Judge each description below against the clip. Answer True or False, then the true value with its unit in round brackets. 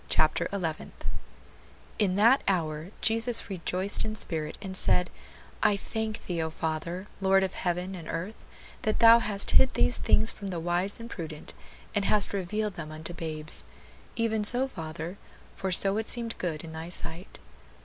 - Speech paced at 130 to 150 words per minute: False (165 wpm)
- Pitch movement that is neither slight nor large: True (4.5 semitones)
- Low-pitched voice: False (190 Hz)